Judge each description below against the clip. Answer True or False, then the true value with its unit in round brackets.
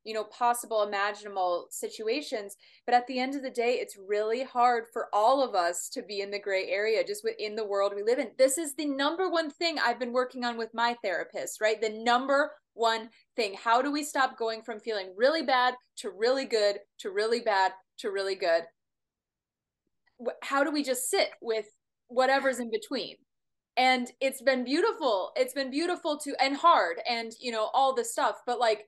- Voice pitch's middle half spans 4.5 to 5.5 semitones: False (4.1 semitones)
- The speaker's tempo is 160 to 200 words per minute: True (195 wpm)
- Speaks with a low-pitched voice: False (245 Hz)